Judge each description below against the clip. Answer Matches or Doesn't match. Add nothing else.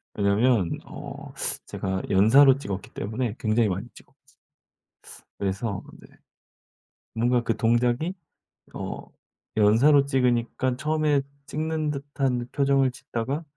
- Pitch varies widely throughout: Doesn't match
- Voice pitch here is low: Matches